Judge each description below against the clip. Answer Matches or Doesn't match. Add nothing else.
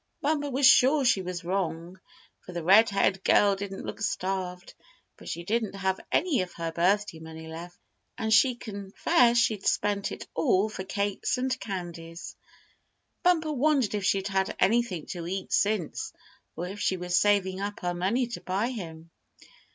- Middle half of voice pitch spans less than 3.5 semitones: Doesn't match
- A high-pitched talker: Matches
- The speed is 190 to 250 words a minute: Doesn't match